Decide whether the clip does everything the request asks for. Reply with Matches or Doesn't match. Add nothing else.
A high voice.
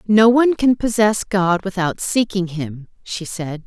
Matches